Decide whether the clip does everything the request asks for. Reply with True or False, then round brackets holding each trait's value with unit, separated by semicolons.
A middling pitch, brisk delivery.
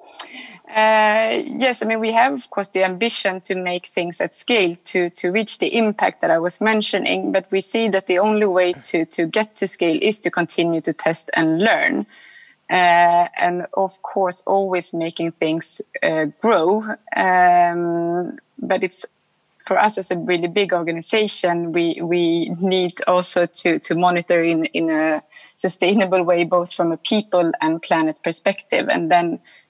False (180 Hz; 170 wpm)